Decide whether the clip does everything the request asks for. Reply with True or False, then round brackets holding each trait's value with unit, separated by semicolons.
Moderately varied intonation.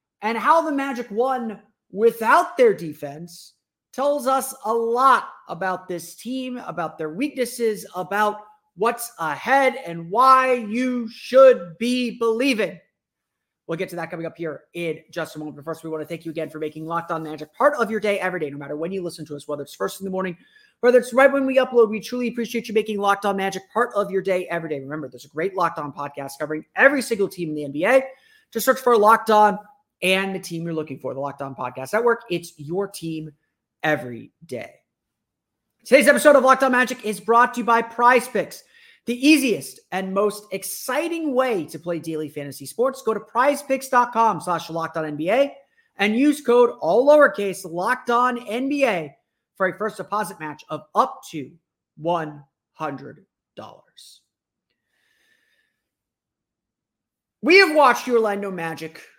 False (7.3 semitones)